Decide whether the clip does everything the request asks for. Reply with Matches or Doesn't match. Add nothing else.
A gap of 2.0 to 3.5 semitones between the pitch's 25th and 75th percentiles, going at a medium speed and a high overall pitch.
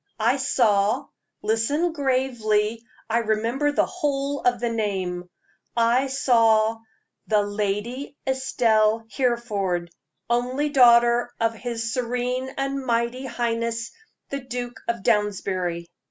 Doesn't match